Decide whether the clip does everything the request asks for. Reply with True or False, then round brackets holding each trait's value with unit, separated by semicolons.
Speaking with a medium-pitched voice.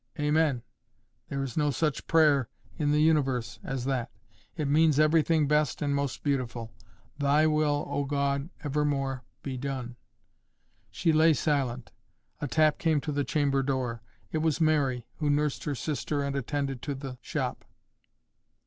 True (145 Hz)